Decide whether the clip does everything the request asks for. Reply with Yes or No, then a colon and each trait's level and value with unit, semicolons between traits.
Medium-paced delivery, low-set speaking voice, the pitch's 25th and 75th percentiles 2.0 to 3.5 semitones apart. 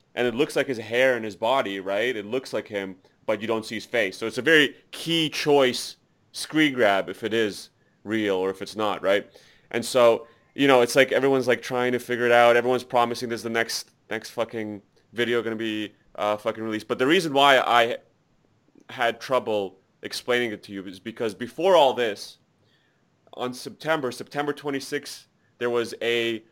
Yes: average, 195 wpm; low, 120 Hz; average, 2.9 semitones